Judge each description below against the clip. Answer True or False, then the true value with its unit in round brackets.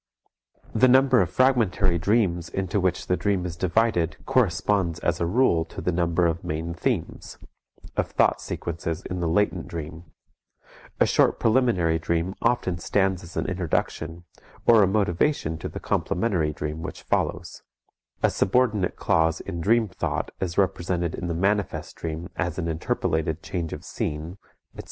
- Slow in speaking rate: False (155 wpm)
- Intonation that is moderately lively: True (3.5 semitones)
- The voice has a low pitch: True (90 Hz)